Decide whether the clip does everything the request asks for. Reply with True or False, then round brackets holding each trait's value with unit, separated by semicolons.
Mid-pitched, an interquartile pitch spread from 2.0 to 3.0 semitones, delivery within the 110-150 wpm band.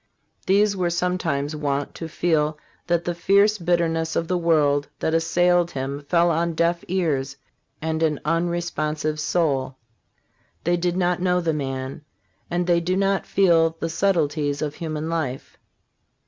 True (165 Hz; 2.6 semitones; 145 wpm)